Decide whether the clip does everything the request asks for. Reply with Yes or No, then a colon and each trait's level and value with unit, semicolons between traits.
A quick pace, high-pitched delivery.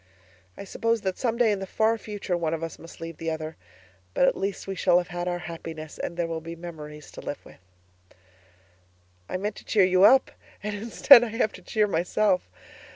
No: fast, 215 wpm; medium, 180 Hz